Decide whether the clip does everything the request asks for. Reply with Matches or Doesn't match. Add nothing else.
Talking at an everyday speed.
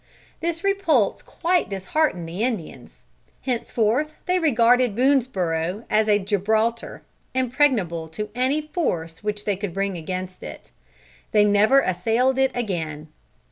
Doesn't match